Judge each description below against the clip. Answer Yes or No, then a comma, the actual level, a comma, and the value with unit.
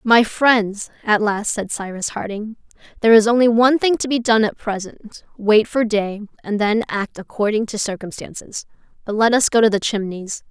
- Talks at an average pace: Yes, average, 190 wpm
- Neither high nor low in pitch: No, high, 215 Hz